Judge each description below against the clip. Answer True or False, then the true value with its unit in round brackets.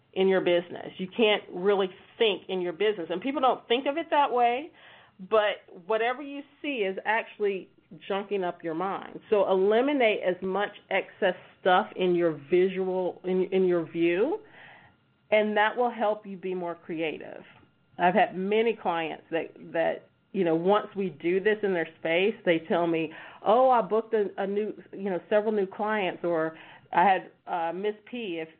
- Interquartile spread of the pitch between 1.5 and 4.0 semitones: True (3.5 semitones)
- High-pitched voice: True (195 Hz)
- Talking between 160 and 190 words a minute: True (180 wpm)